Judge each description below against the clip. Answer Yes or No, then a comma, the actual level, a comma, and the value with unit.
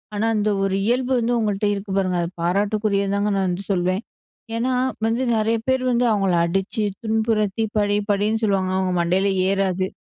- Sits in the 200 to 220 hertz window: Yes, high, 205 Hz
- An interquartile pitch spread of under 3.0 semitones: Yes, narrow, 2.4 semitones